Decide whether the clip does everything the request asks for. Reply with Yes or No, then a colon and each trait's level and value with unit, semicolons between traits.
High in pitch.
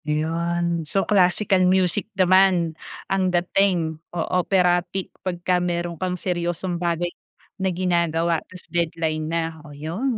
No: medium, 175 Hz